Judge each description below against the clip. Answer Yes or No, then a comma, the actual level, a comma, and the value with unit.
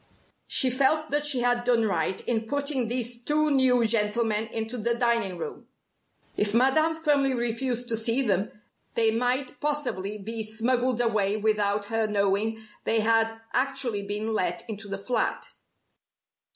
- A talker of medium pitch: No, high, 230 Hz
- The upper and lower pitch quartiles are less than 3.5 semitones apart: Yes, average, 3.0 semitones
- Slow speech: No, average, 150 wpm